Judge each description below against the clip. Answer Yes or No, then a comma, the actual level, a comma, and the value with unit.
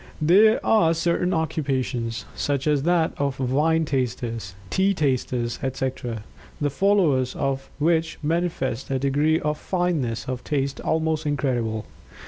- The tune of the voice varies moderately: Yes, average, 4.0 semitones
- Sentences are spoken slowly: Yes, slow, 125 wpm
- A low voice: No, medium, 145 Hz